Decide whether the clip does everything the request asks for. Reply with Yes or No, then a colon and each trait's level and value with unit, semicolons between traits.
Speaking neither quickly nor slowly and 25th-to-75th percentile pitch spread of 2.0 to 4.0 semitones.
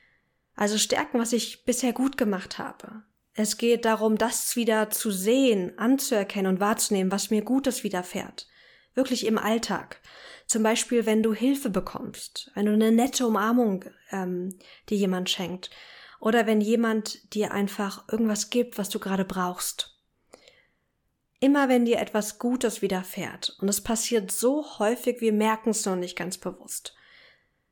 Yes: average, 150 wpm; average, 2.9 semitones